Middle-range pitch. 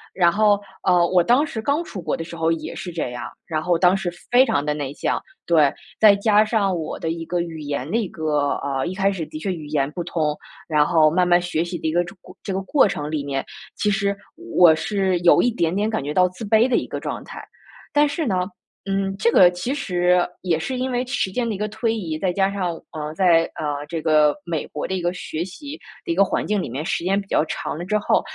Yes: medium, 180 Hz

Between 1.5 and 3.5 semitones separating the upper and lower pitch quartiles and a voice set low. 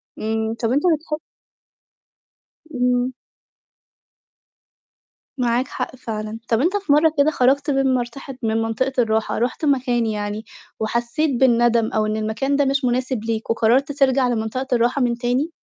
No: average, 3.2 semitones; high, 245 Hz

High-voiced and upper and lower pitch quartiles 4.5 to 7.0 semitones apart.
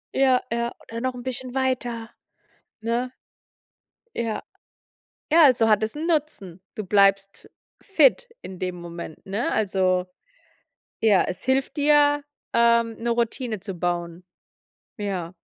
Yes: high, 230 Hz; average, 5.0 semitones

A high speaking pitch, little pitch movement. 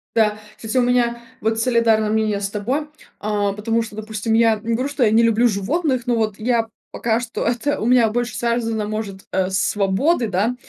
Yes: high, 225 Hz; narrow, 2.2 semitones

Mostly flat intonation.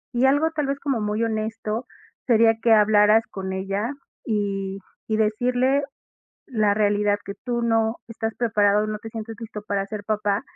Yes: narrow, 2.1 semitones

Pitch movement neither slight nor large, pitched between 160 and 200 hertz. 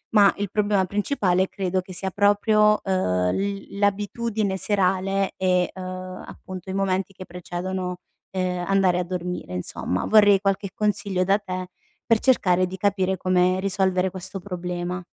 No: narrow, 1.7 semitones; high, 190 Hz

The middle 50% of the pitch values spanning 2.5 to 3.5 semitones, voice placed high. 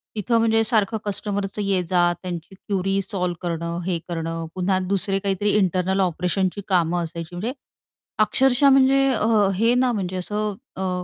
Yes: average, 3.0 semitones; high, 195 Hz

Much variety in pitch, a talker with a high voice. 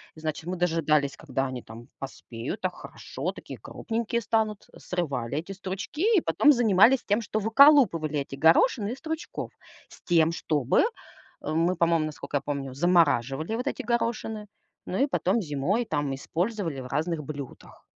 No: wide, 7.1 semitones; medium, 170 Hz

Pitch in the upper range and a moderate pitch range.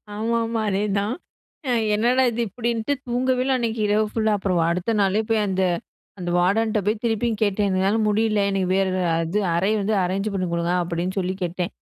Yes: high, 210 Hz; average, 3.1 semitones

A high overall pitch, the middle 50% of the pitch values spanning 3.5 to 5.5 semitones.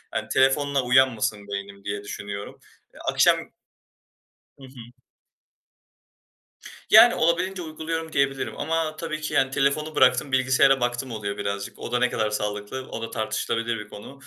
No: low, 130 Hz; average, 5.2 semitones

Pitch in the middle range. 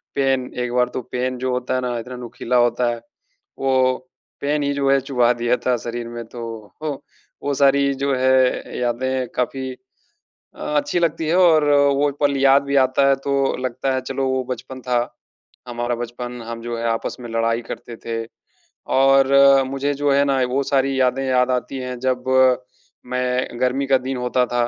No: low, 130 Hz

